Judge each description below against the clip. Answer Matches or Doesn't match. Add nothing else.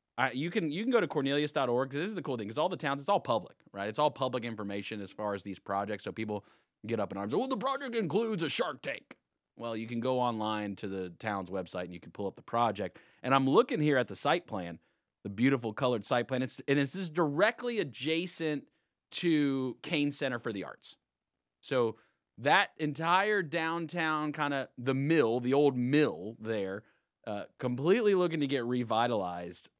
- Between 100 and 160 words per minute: Doesn't match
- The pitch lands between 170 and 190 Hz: Doesn't match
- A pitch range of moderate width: Doesn't match